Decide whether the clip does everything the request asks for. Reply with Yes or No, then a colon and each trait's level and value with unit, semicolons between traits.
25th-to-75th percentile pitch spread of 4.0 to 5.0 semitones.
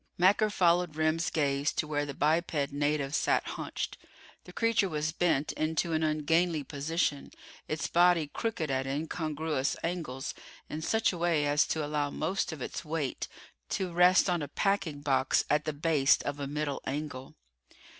No: average, 2.9 semitones